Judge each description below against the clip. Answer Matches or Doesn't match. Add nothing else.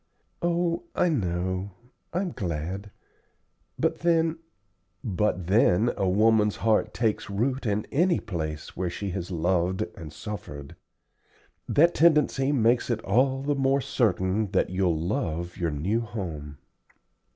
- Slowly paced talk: Matches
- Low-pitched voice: Matches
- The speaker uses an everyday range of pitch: Doesn't match